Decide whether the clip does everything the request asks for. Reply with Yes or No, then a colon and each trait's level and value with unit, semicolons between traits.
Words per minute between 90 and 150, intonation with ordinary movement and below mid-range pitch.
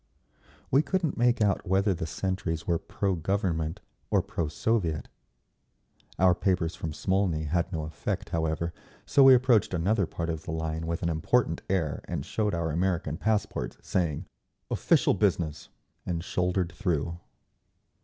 Yes: average, 145 wpm; average, 3.4 semitones; very low, 85 Hz